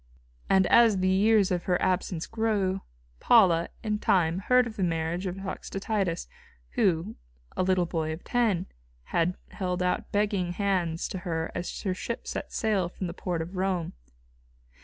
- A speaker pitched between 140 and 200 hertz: Yes, medium, 185 Hz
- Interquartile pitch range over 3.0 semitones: No, average, 2.7 semitones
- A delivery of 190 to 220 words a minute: No, average, 160 wpm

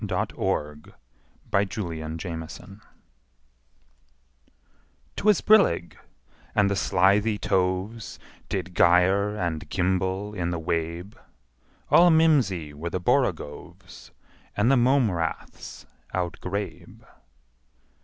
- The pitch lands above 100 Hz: No, very low, 95 Hz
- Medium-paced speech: No, slow, 85 wpm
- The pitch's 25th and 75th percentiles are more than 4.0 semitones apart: No, average, 3.5 semitones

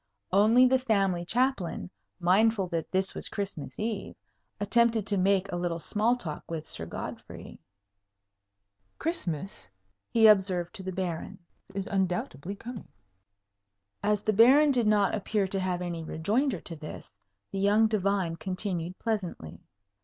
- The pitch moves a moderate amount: Yes, average, 3.8 semitones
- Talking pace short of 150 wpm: Yes, average, 140 wpm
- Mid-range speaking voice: No, high, 195 Hz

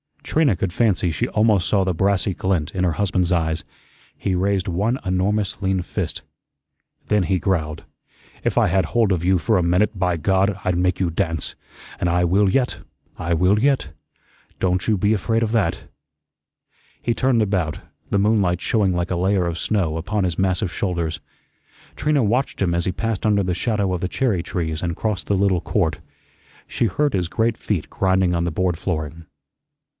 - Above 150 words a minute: Yes, average, 185 wpm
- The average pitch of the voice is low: Yes, very low, 95 Hz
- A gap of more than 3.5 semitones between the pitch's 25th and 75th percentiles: No, average, 3.0 semitones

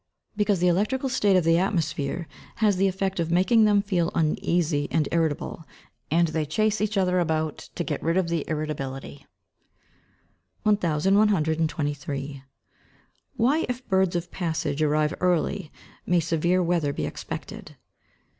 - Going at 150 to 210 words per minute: No, average, 140 wpm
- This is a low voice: No, medium, 170 Hz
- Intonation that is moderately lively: Yes, average, 3.9 semitones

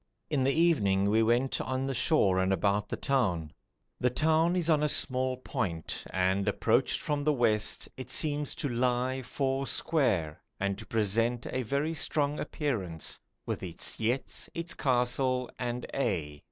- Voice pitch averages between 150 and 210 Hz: No, low, 125 Hz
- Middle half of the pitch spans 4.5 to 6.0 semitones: Yes, wide, 5.4 semitones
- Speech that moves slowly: No, average, 160 wpm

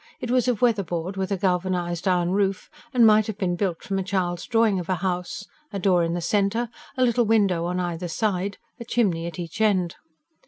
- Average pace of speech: No, fast, 220 wpm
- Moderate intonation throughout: Yes, average, 3.4 semitones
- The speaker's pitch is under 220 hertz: Yes, high, 190 Hz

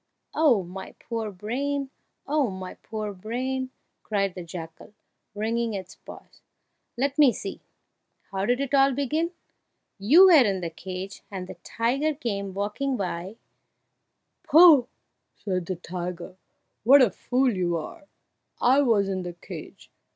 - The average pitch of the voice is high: Yes, high, 215 Hz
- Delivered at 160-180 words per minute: No, average, 145 wpm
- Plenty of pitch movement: Yes, wide, 6.3 semitones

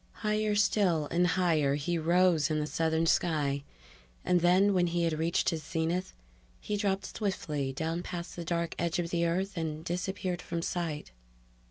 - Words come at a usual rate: Yes, average, 170 wpm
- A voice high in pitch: No, medium, 170 Hz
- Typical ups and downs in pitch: No, narrow, 2.2 semitones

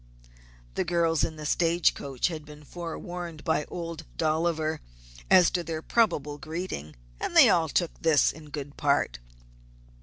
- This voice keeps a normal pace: Yes, average, 150 wpm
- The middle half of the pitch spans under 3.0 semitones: Yes, narrow, 2.4 semitones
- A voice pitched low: No, medium, 160 Hz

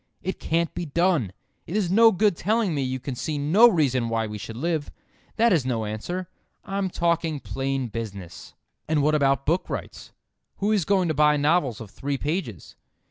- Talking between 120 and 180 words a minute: No, average, 190 wpm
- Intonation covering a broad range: Yes, wide, 5.7 semitones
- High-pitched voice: No, medium, 150 Hz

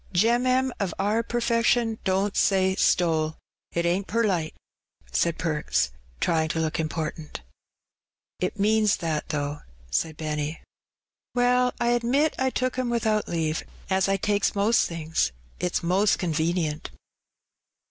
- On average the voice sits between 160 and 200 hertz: Yes, high, 190 Hz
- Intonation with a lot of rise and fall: Yes, wide, 6.2 semitones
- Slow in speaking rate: Yes, slow, 130 wpm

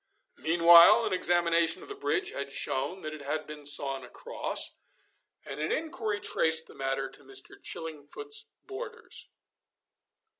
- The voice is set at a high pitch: No, medium, 165 Hz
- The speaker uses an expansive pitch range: Yes, wide, 7.8 semitones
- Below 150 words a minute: Yes, average, 140 wpm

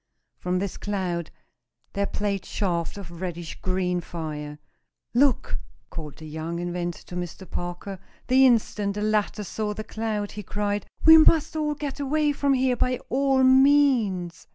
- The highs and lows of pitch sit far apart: Yes, wide, 6.5 semitones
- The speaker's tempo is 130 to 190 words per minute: Yes, average, 150 wpm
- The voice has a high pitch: Yes, high, 205 Hz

